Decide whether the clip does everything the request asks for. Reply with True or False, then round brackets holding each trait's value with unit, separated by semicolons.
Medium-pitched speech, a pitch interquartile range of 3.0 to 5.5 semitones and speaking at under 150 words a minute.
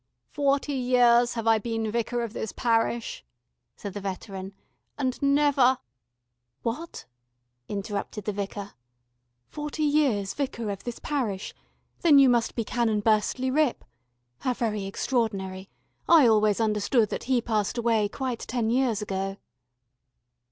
False (230 Hz; 3.9 semitones; 135 wpm)